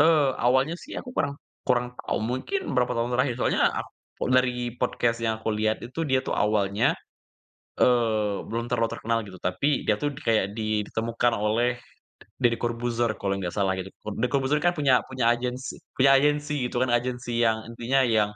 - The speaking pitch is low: Yes, low, 120 Hz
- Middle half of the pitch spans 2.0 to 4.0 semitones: Yes, average, 2.7 semitones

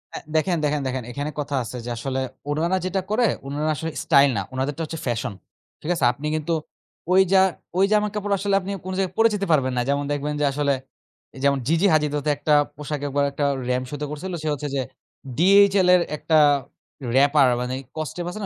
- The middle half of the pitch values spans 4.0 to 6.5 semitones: Yes, average, 4.7 semitones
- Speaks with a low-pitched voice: No, medium, 150 Hz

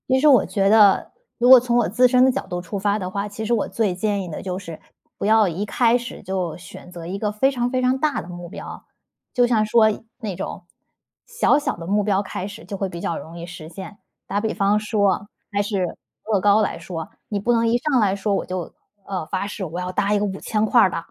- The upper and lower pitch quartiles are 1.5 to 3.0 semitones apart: No, average, 3.7 semitones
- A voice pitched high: Yes, high, 205 Hz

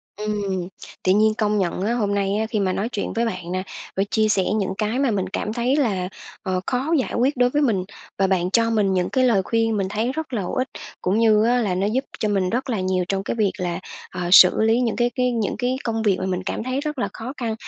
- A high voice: Yes, high, 215 Hz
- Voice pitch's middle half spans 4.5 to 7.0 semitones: No, average, 3.9 semitones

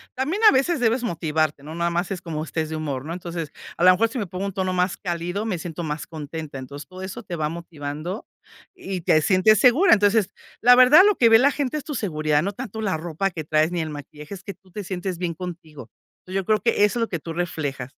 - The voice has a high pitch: No, medium, 180 Hz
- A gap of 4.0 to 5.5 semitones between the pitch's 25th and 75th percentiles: Yes, average, 5.2 semitones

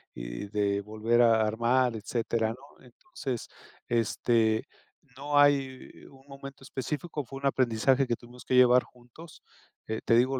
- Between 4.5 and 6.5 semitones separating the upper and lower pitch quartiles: No, average, 3.3 semitones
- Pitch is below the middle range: Yes, low, 125 Hz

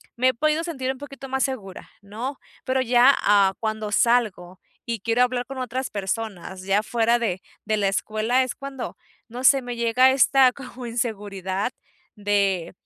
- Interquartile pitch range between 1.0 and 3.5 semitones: No, average, 4.0 semitones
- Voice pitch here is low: No, high, 235 Hz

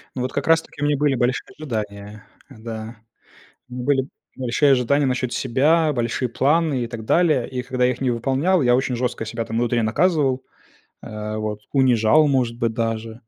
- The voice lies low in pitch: Yes, low, 125 Hz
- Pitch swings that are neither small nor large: Yes, average, 3.3 semitones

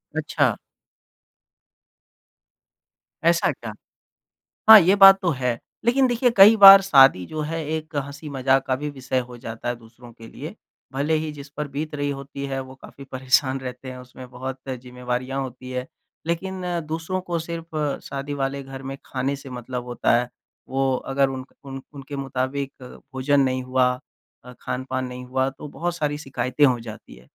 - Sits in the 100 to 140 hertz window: Yes, low, 135 Hz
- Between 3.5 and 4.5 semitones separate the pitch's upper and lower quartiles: No, average, 2.7 semitones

